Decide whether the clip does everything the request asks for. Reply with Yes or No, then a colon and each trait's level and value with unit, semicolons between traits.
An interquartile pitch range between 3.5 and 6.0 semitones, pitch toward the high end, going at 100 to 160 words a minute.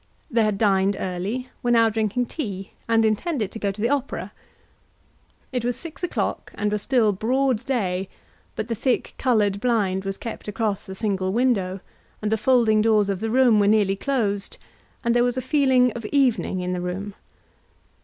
No: average, 3.8 semitones; high, 220 Hz; average, 185 wpm